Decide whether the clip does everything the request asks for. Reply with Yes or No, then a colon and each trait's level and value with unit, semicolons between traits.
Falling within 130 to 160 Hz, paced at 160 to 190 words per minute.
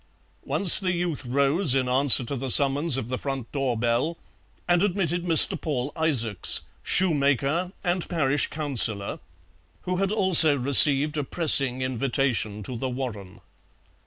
No: medium, 140 Hz; average, 140 wpm